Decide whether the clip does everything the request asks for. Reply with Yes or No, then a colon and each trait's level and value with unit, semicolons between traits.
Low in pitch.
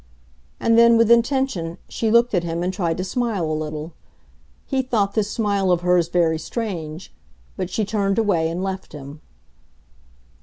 No: high, 190 Hz